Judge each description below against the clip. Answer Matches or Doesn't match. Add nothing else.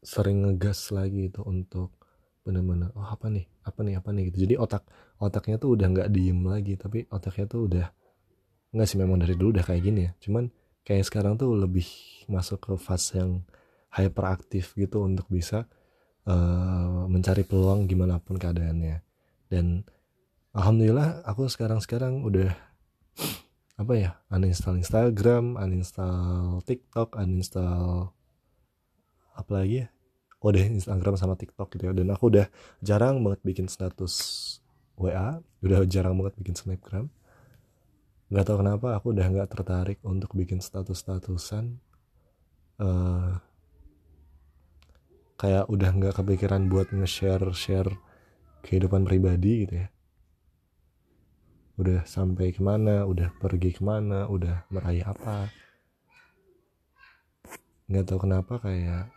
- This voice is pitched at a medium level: Doesn't match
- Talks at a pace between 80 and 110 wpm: Doesn't match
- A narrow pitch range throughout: Matches